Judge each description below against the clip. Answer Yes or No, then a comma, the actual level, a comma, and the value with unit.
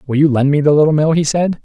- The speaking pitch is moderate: Yes, medium, 150 Hz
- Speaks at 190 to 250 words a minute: No, fast, 330 wpm